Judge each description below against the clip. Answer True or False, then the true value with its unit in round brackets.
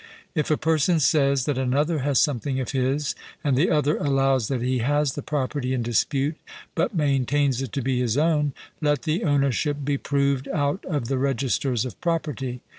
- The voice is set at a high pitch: False (140 Hz)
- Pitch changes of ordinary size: False (2.2 semitones)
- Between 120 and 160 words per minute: False (185 wpm)